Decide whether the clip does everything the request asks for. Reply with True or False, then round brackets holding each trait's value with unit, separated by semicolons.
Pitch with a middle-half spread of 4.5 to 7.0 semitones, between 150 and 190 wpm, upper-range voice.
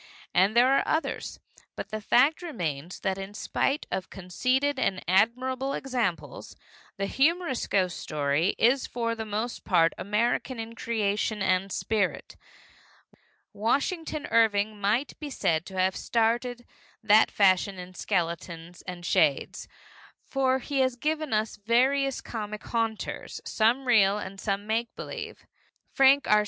False (5.2 semitones; 135 wpm; 220 Hz)